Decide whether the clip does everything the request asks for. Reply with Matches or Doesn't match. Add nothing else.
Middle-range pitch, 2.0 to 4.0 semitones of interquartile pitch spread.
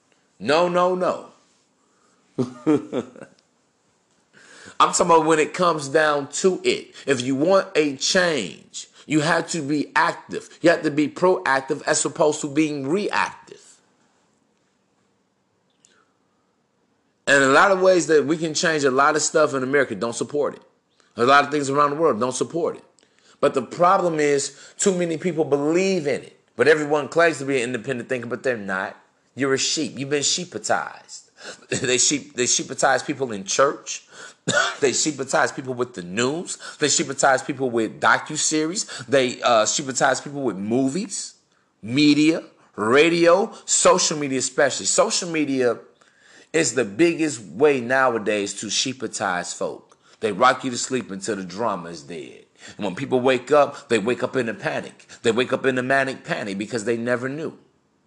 Doesn't match